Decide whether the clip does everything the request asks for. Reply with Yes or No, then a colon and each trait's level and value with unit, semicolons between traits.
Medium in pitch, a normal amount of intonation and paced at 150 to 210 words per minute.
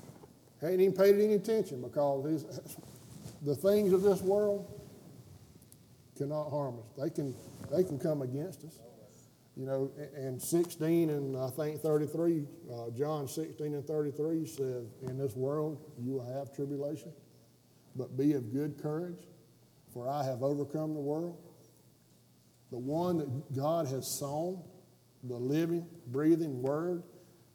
No: medium, 145 Hz; average, 3.7 semitones; average, 140 wpm